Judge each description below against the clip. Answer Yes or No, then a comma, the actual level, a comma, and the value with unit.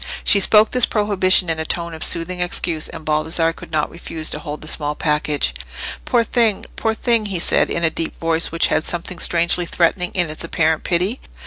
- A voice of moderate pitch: Yes, medium, 170 Hz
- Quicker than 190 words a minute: Yes, fast, 205 wpm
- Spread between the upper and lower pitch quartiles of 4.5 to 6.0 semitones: No, average, 2.8 semitones